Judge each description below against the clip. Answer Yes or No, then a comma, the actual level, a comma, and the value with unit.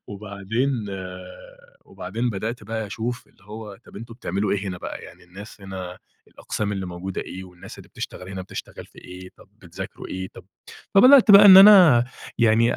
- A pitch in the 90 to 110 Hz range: Yes, low, 105 Hz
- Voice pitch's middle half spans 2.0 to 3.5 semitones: No, average, 3.9 semitones